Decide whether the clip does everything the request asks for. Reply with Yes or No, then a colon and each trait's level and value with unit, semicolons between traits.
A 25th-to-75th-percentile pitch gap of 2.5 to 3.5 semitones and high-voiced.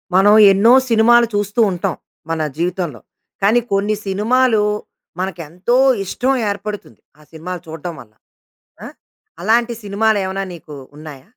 No: average, 4.1 semitones; high, 195 Hz